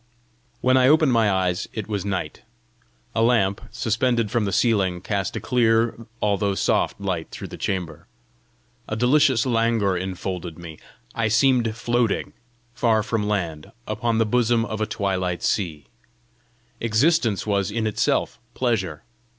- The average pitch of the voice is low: Yes, low, 110 Hz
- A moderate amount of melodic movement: Yes, average, 3.4 semitones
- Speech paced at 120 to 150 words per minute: Yes, average, 140 wpm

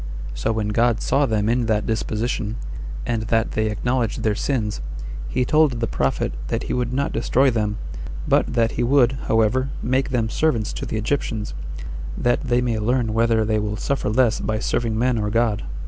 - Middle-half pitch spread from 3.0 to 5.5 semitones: No, narrow, 2.4 semitones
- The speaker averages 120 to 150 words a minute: No, average, 185 wpm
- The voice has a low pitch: Yes, low, 115 Hz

